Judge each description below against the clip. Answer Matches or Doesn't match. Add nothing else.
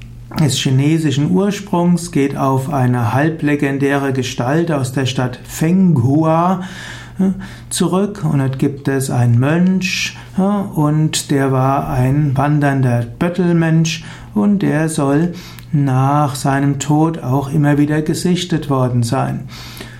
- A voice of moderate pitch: Matches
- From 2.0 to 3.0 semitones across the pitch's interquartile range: Doesn't match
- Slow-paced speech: Matches